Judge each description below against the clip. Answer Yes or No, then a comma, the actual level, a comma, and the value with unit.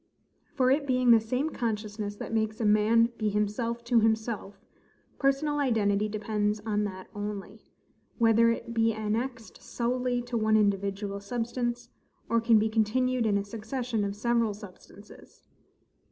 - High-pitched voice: Yes, high, 225 Hz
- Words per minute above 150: No, average, 145 wpm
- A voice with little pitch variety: Yes, narrow, 2.3 semitones